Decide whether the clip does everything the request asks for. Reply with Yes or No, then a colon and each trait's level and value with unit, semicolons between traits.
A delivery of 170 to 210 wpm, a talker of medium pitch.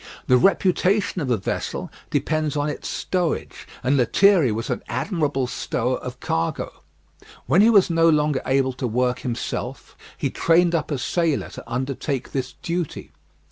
No: average, 155 wpm; medium, 145 Hz